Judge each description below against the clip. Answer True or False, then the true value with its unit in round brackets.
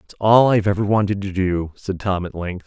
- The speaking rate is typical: False (250 wpm)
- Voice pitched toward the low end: True (100 Hz)